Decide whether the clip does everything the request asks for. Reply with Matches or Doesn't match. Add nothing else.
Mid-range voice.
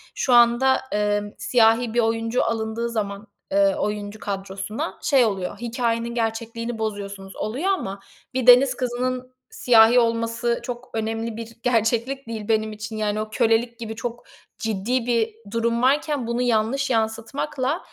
Doesn't match